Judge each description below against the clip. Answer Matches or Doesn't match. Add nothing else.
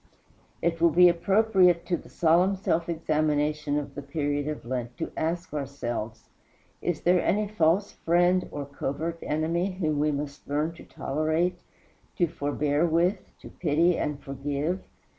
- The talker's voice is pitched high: Doesn't match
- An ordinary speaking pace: Matches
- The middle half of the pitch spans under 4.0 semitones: Matches